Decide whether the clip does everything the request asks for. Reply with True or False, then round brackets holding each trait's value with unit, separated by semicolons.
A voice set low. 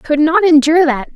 False (310 Hz)